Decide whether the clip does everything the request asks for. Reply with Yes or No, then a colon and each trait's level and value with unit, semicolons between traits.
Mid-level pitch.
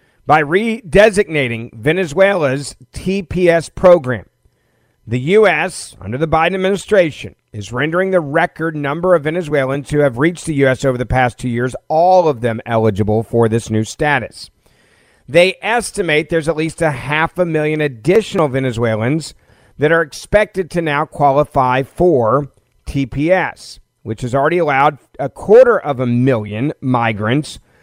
Yes: medium, 145 Hz